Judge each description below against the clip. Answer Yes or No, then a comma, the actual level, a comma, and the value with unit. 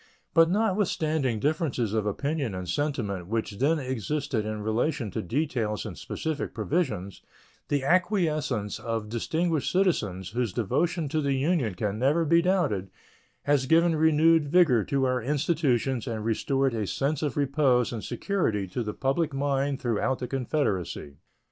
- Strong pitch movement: Yes, wide, 6.2 semitones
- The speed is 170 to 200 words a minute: No, average, 150 wpm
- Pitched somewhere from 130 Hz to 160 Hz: Yes, low, 135 Hz